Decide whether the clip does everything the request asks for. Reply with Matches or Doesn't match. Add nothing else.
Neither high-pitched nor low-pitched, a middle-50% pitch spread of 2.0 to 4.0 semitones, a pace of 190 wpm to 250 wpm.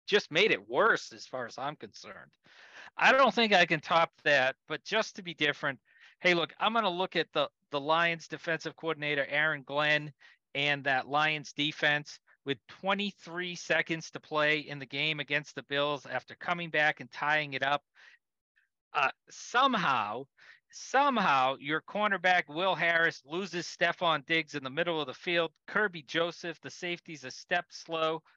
Doesn't match